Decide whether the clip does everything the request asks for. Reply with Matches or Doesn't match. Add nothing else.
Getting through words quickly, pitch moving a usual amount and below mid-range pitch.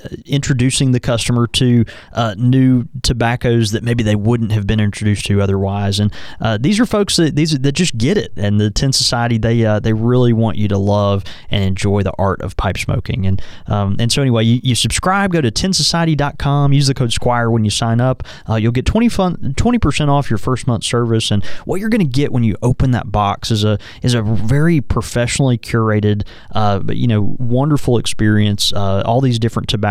Matches